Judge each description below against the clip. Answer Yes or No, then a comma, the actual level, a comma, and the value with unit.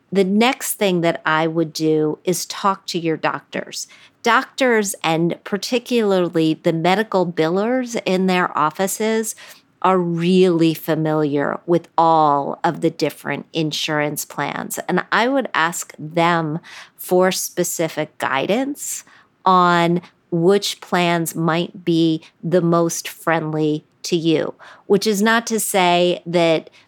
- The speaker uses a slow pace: Yes, slow, 125 wpm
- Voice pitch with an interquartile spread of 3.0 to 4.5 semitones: Yes, average, 3.3 semitones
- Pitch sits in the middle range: Yes, medium, 170 Hz